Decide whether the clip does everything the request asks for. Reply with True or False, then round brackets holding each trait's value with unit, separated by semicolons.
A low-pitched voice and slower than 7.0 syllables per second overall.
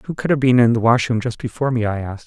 False (120 Hz; 7.2 syllables/s)